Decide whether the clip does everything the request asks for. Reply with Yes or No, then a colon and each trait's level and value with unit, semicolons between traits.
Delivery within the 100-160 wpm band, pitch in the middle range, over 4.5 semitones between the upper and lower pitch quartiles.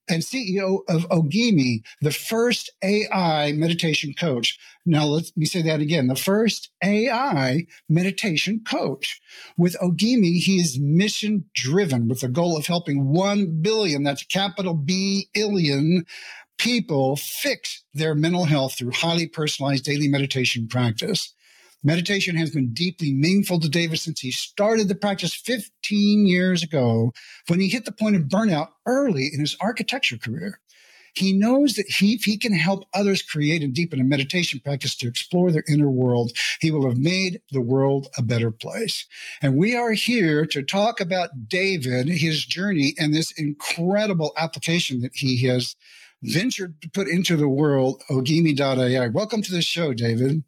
Yes: average, 155 wpm; medium, 165 Hz; wide, 5.6 semitones